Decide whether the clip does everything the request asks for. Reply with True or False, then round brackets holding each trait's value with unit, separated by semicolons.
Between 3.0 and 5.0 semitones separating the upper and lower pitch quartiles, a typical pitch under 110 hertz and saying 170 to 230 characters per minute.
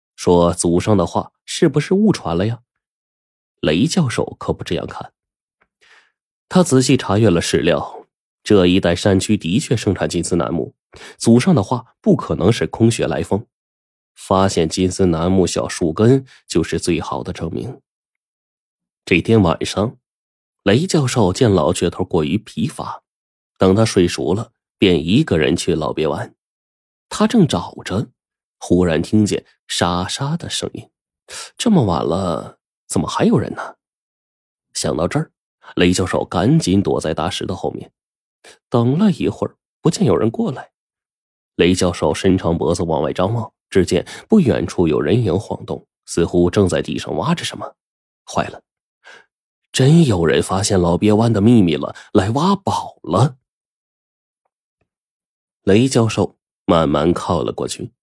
False (5.5 semitones; 95 Hz; 210 characters per minute)